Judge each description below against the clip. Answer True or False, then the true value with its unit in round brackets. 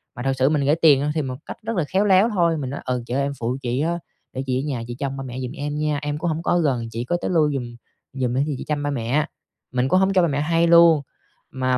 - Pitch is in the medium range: True (145 Hz)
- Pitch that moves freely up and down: False (4.3 semitones)